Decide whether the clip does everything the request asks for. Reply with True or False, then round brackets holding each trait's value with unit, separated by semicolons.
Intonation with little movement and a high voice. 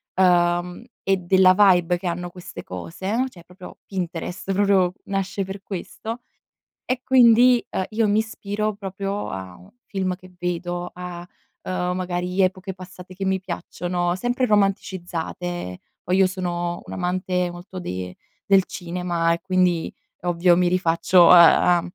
False (1.7 semitones; 180 Hz)